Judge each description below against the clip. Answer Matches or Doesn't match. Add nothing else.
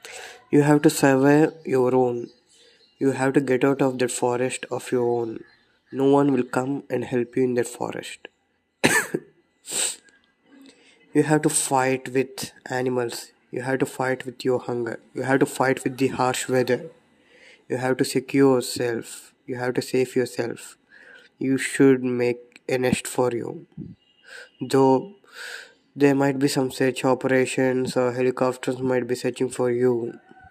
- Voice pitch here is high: Doesn't match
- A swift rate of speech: Matches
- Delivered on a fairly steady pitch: Matches